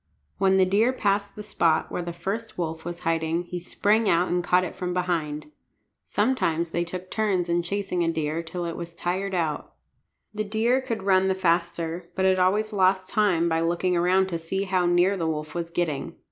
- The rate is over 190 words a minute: Yes, average, 200 wpm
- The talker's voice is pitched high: No, medium, 180 Hz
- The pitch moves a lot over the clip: No, narrow, 2.4 semitones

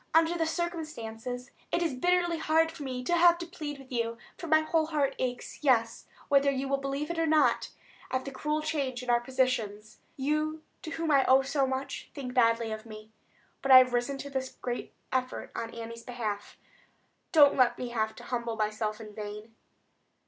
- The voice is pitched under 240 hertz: No, very high, 265 Hz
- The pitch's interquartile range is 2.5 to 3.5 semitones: No, average, 4.6 semitones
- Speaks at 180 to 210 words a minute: Yes, average, 190 wpm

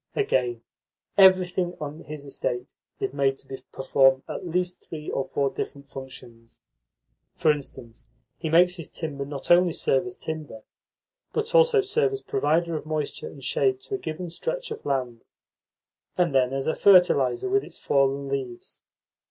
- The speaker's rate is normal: Yes, average, 160 wpm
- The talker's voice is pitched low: No, medium, 155 Hz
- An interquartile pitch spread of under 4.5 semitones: No, average, 5.2 semitones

